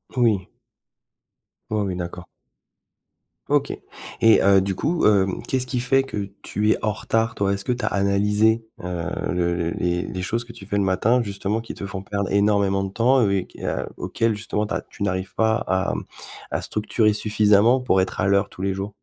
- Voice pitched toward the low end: Yes, low, 100 Hz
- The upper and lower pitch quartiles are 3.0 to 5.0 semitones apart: No, narrow, 2.6 semitones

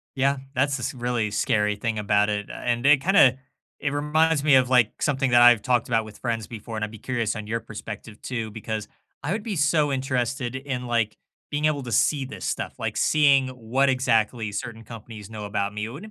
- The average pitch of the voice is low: Yes, low, 120 Hz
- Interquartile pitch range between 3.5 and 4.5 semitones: Yes, average, 3.8 semitones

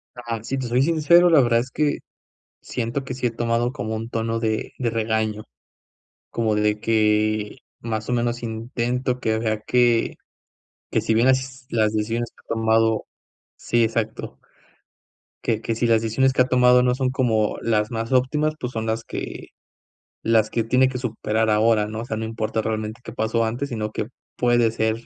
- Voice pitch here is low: Yes, low, 115 Hz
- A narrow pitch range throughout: Yes, narrow, 2.1 semitones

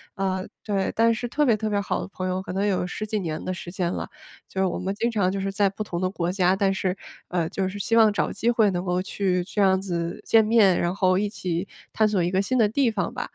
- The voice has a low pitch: No, high, 195 Hz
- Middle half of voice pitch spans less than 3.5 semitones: Yes, narrow, 2.4 semitones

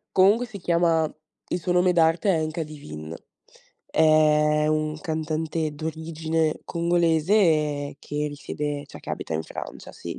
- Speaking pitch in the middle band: Yes, medium, 160 Hz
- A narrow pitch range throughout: Yes, narrow, 1.8 semitones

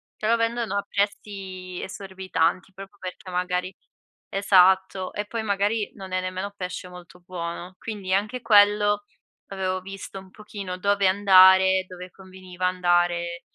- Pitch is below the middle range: No, high, 190 Hz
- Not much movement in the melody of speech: Yes, narrow, 1.7 semitones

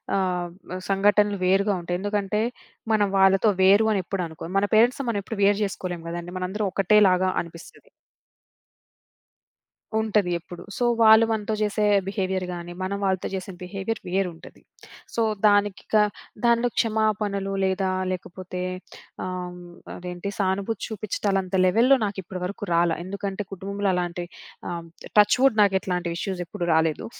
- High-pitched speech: Yes, high, 195 Hz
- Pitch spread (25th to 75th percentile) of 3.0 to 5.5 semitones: No, narrow, 2.4 semitones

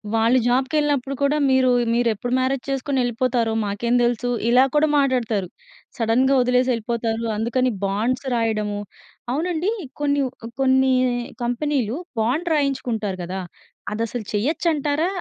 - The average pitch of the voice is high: Yes, very high, 250 Hz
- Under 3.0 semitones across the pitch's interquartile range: No, average, 3.4 semitones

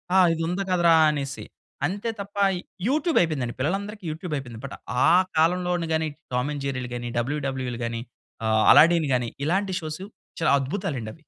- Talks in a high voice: No, medium, 155 Hz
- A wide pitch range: Yes, wide, 5.8 semitones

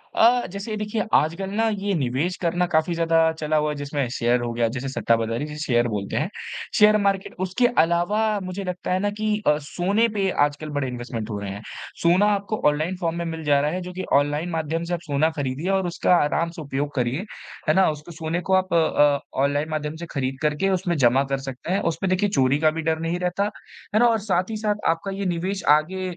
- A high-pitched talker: No, medium, 165 Hz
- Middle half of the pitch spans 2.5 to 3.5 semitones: No, average, 4.6 semitones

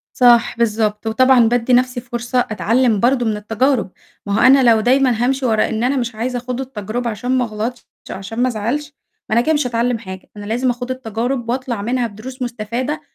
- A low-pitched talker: No, high, 240 Hz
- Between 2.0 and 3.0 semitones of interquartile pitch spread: Yes, narrow, 2.4 semitones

